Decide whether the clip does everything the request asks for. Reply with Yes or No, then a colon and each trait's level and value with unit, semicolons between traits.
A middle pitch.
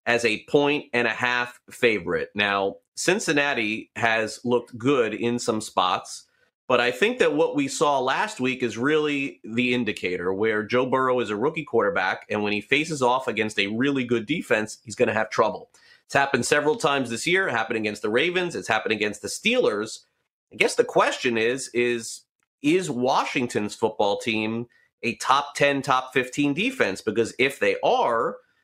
No: low, 125 Hz